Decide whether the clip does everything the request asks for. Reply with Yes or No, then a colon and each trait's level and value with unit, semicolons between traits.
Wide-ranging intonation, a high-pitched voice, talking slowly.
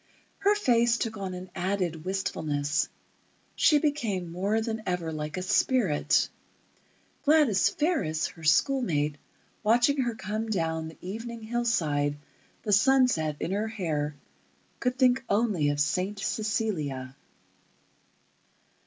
Yes: wide, 6.7 semitones; high, 200 Hz; slow, 120 wpm